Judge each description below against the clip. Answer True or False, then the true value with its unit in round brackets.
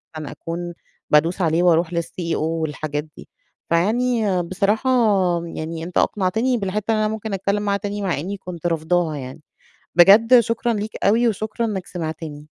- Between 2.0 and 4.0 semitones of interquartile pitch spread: False (4.5 semitones)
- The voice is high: False (180 Hz)